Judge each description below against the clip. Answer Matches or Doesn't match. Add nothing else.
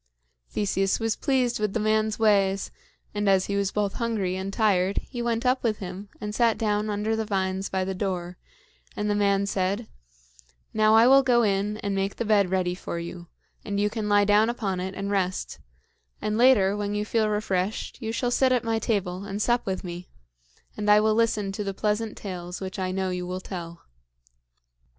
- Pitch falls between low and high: Doesn't match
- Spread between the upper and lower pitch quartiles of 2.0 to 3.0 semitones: Matches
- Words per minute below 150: Doesn't match